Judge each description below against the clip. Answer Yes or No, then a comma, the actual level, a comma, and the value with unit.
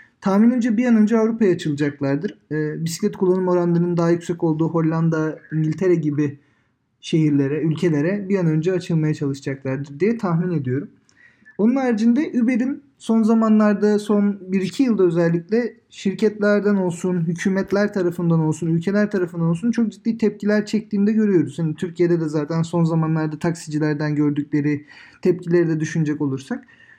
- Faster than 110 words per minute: Yes, average, 135 wpm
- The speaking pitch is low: No, medium, 175 Hz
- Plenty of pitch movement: No, average, 4.9 semitones